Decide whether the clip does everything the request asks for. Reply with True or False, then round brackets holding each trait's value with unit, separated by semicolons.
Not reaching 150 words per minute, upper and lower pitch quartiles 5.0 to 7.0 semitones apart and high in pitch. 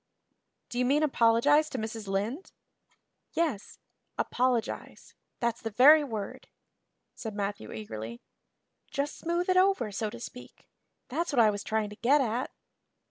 True (140 wpm; 5.6 semitones; 235 Hz)